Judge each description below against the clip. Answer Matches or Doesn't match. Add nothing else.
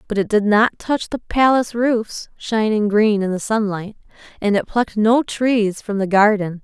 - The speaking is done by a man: Doesn't match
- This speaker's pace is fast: Doesn't match